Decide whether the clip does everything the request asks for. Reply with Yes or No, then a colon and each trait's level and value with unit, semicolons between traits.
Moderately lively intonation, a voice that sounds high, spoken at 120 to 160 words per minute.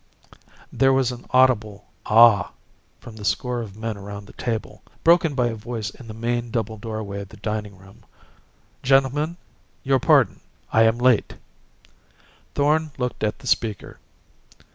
No: average, 3.2 semitones; low, 115 Hz; average, 150 wpm